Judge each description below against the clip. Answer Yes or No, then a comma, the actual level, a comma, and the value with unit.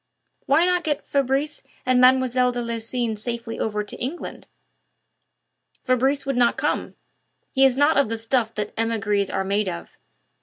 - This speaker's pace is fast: No, average, 155 wpm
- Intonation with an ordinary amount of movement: Yes, average, 3.3 semitones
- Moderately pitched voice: No, high, 245 Hz